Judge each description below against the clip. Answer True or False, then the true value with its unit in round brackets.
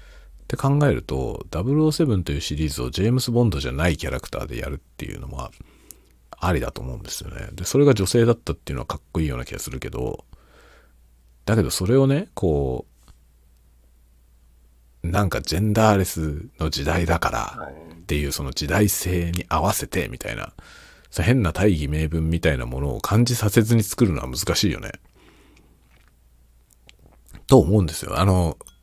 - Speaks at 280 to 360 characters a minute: True (335 characters per minute)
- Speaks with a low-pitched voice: True (80 Hz)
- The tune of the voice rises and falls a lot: True (8.3 semitones)